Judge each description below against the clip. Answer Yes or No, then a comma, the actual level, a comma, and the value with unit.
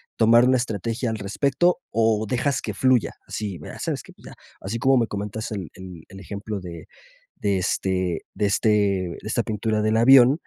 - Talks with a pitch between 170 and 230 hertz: No, low, 110 Hz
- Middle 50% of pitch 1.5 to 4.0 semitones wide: Yes, average, 3.2 semitones